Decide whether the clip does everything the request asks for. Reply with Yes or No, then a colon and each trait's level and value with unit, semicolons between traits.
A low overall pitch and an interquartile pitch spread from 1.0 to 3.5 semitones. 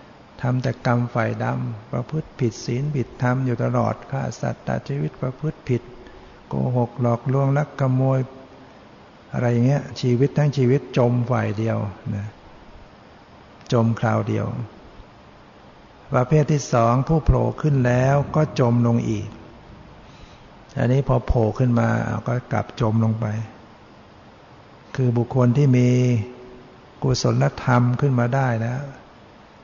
Yes: low, 125 Hz; narrow, 2.5 semitones